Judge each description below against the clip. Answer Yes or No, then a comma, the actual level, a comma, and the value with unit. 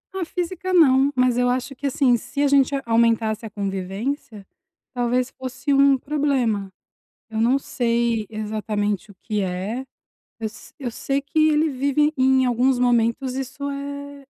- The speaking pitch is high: Yes, very high, 255 Hz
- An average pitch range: Yes, average, 3.9 semitones